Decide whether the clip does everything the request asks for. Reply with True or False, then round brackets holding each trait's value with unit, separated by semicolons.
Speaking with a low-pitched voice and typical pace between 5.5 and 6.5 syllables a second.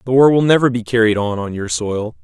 True (115 Hz; 5.9 syllables/s)